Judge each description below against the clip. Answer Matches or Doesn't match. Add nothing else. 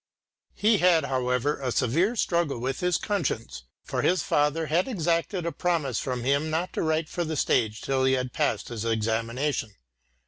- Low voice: Doesn't match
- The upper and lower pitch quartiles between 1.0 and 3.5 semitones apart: Doesn't match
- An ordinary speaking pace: Matches